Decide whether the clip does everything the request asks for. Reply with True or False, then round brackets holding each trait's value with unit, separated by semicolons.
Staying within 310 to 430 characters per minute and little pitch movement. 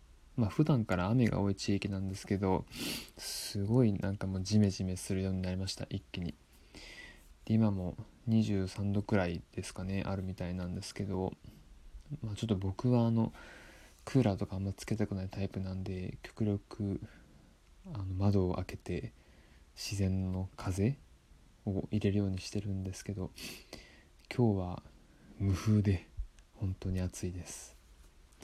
False (285 characters per minute; 2.2 semitones)